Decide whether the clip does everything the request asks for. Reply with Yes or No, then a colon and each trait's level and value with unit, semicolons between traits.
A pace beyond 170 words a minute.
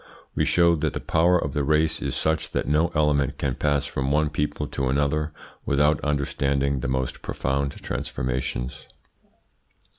No: average, 155 wpm